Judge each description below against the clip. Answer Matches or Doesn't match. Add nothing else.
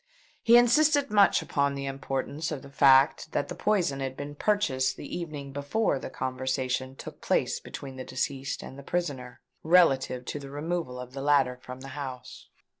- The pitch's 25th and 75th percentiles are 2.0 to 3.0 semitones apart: Doesn't match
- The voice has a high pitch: Doesn't match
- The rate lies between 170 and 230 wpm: Matches